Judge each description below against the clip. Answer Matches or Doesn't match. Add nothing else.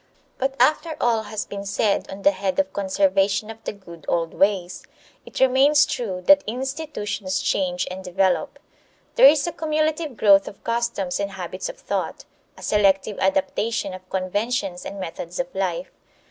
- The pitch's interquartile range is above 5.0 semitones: Matches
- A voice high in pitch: Matches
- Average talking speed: Matches